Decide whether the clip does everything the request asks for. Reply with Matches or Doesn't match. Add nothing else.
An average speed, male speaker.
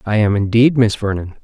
Doesn't match